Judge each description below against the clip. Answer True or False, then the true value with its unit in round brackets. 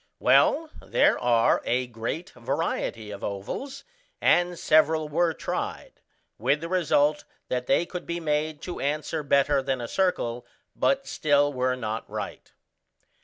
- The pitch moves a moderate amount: True (5.0 semitones)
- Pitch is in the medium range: True (145 Hz)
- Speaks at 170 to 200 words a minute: False (140 wpm)